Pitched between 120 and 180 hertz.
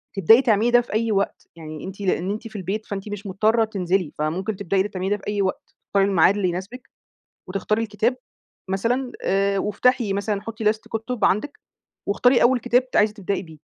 No: high, 205 Hz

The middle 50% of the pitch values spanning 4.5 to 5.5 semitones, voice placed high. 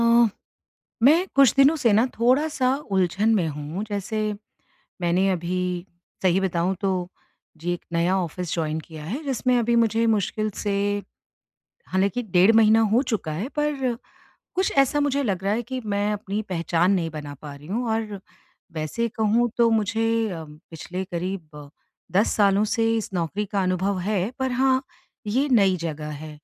Yes: average, 5.0 semitones; high, 200 Hz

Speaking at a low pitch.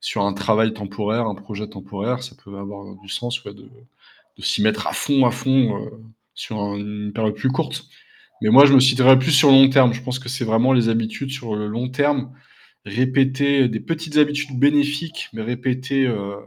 Yes: low, 125 Hz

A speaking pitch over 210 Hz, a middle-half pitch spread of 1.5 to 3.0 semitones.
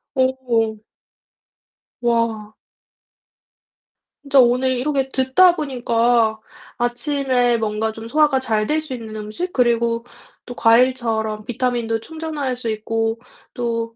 Yes: high, 240 Hz; narrow, 2.6 semitones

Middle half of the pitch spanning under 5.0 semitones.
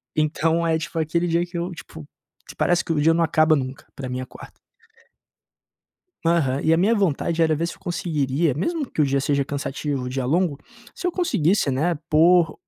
Yes: average, 3.3 semitones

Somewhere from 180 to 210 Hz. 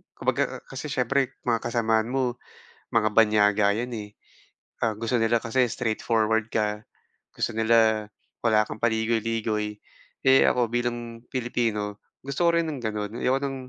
No: low, 115 Hz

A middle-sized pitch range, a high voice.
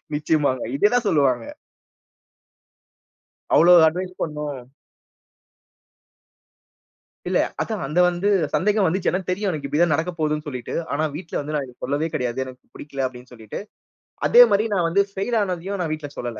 No: average, 4.8 semitones; medium, 155 Hz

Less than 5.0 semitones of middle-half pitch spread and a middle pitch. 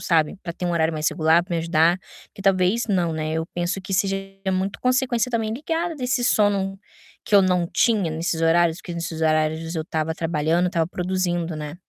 Yes: average, 3.2 semitones; medium, 175 Hz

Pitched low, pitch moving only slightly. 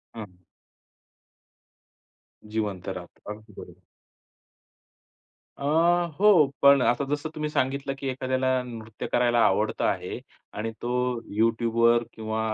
No: low, 120 Hz; average, 4.2 semitones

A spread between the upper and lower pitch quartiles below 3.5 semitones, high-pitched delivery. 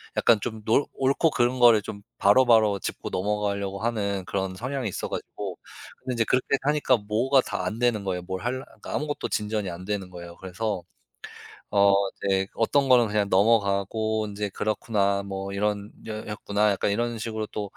No: average, 2.9 semitones; low, 105 Hz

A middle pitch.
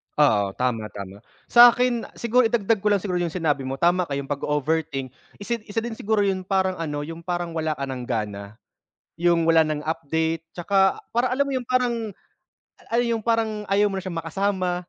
Yes: medium, 175 Hz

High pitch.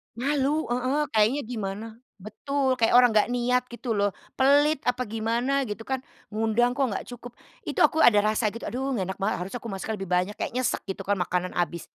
Yes: high, 235 Hz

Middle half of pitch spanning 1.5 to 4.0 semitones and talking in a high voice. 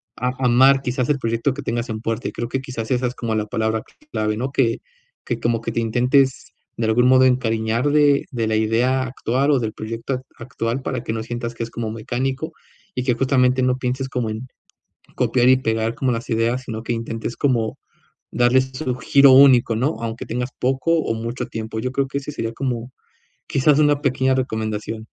No: narrow, 2.5 semitones; low, 125 Hz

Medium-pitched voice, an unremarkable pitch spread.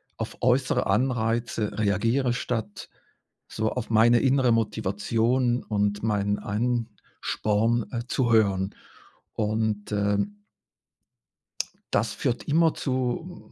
No: low, 115 Hz; average, 3.0 semitones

